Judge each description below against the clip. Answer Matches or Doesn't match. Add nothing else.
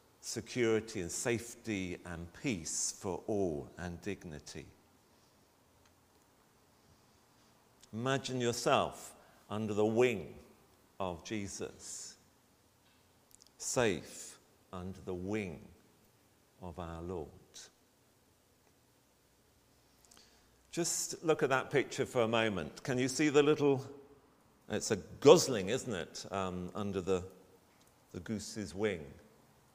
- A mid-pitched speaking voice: Doesn't match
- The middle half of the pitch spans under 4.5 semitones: Doesn't match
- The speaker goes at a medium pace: Doesn't match